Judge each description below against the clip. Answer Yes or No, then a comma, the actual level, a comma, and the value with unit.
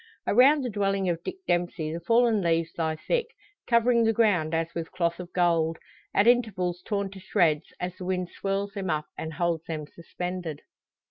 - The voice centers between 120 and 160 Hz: No, medium, 180 Hz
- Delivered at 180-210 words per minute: Yes, average, 185 wpm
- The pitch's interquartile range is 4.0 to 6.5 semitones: No, average, 3.6 semitones